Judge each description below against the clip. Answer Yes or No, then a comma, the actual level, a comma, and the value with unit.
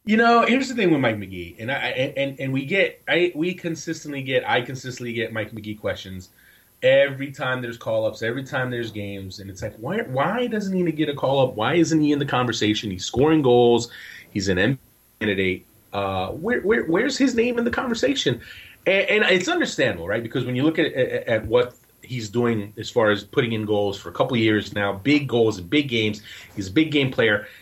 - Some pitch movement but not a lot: No, wide, 7.1 semitones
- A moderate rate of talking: No, fast, 220 wpm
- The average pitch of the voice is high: No, low, 125 Hz